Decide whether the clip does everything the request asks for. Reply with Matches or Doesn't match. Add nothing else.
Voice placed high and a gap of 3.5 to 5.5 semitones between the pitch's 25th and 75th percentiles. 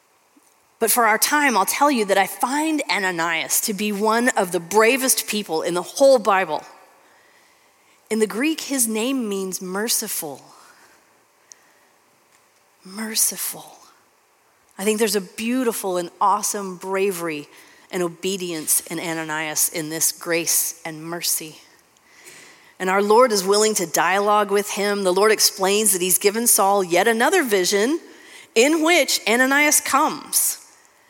Matches